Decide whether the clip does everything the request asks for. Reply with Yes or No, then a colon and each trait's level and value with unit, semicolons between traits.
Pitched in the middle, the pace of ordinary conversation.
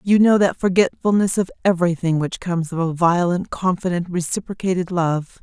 Yes: medium, 180 Hz; average, 155 wpm